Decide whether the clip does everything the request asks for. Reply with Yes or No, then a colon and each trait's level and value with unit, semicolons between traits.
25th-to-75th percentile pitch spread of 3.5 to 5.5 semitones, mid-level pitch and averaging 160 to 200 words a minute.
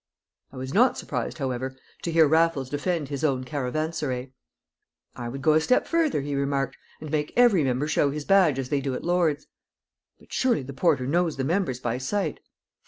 Yes: average, 4.0 semitones; medium, 145 Hz; average, 190 wpm